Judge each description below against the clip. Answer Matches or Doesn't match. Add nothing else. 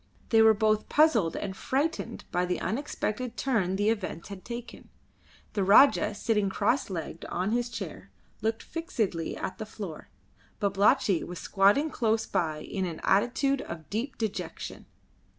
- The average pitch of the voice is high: Matches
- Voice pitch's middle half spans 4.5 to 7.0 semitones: Doesn't match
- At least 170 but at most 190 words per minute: Doesn't match